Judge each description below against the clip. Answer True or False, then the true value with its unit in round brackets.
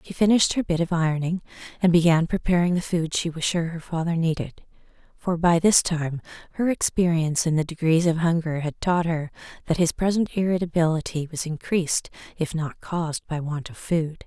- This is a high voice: False (165 Hz)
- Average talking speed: True (185 wpm)